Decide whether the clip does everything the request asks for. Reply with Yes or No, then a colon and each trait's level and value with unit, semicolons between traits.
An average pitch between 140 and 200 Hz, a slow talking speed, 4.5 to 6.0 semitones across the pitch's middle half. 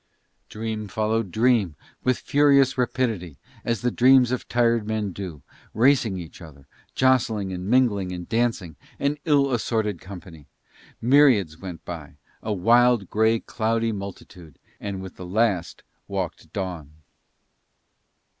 No: low, 105 Hz; slow, 125 wpm; average, 4.9 semitones